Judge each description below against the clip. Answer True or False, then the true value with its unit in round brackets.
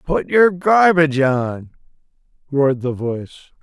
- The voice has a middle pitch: True (145 Hz)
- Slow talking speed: True (115 wpm)